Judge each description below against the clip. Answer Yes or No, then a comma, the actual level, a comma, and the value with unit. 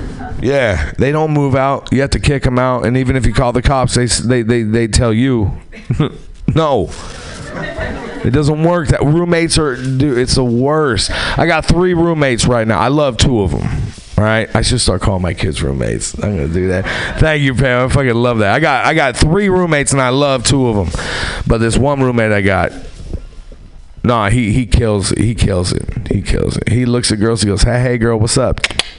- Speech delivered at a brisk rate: Yes, fast, 220 wpm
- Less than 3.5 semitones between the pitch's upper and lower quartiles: No, average, 3.9 semitones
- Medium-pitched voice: No, low, 120 Hz